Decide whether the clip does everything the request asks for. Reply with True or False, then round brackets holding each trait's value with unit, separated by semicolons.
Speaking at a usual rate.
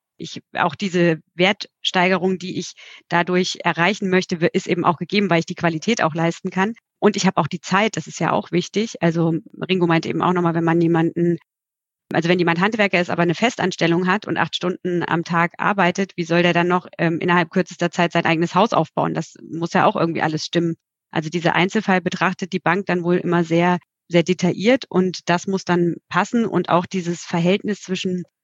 False (205 wpm)